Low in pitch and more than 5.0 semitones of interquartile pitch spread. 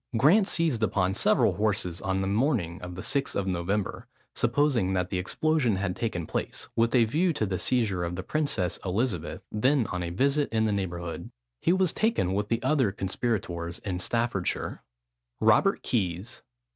Yes: low, 105 Hz; wide, 5.6 semitones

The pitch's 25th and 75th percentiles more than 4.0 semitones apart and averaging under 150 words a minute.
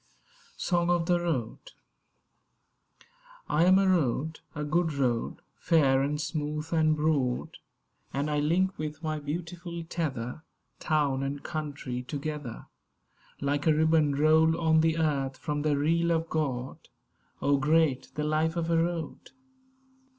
No: narrow, 2.4 semitones; slow, 135 wpm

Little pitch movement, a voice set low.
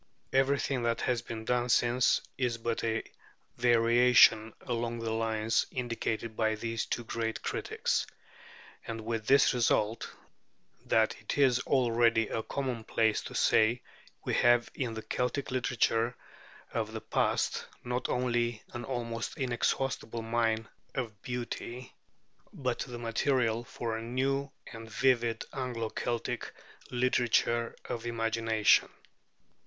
Yes: narrow, 1.6 semitones; low, 120 Hz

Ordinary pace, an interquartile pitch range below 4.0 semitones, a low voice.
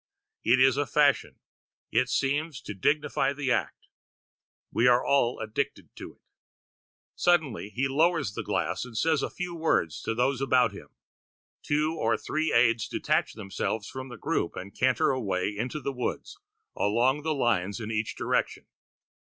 No: average, 160 wpm; average, 4.5 semitones; low, 130 Hz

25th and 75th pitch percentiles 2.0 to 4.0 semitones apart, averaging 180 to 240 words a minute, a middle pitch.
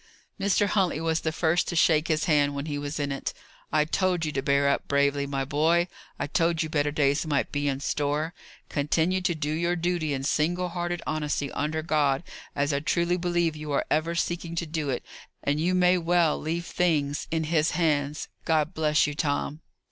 Yes: average, 2.9 semitones; average, 200 wpm; medium, 155 Hz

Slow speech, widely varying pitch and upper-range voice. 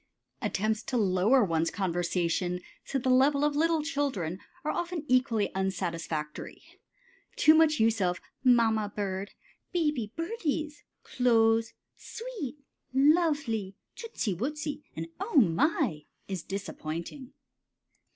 Yes: slow, 110 wpm; wide, 7.8 semitones; high, 230 Hz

